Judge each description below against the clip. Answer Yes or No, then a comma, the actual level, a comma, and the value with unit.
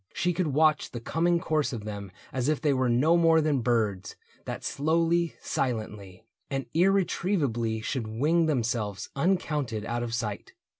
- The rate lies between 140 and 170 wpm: Yes, average, 155 wpm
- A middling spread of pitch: No, wide, 6.3 semitones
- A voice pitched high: No, low, 135 Hz